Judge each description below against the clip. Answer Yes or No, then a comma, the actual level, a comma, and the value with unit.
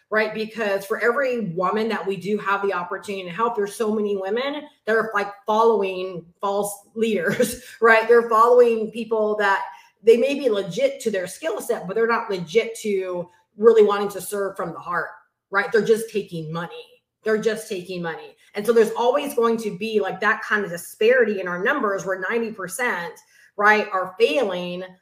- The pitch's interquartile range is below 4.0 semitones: Yes, average, 2.9 semitones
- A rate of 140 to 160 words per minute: No, average, 185 wpm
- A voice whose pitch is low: No, high, 210 Hz